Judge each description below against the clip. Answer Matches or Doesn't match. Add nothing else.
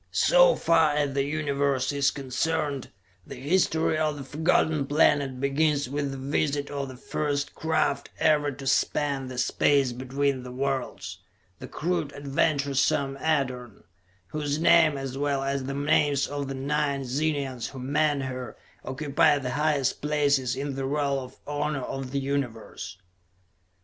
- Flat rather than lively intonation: Matches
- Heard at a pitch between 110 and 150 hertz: Matches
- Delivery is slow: Doesn't match